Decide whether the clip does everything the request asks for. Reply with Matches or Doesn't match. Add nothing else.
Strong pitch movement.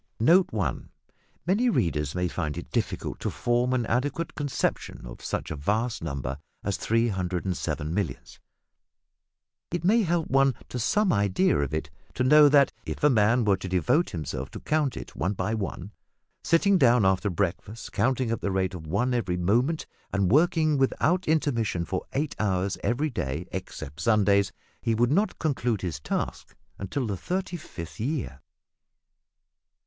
Matches